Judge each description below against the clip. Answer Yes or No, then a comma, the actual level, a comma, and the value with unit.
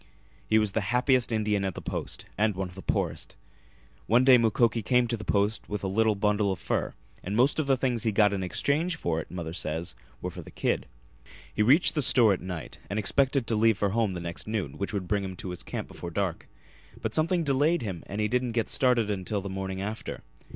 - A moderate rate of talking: No, fast, 235 wpm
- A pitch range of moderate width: Yes, average, 4.0 semitones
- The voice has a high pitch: No, low, 105 Hz